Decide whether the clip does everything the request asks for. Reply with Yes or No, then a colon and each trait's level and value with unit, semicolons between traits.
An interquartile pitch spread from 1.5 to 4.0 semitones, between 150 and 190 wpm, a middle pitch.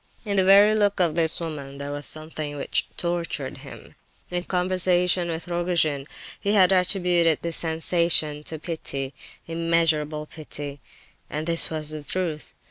No: average, 2.8 semitones; average, 140 wpm; medium, 165 Hz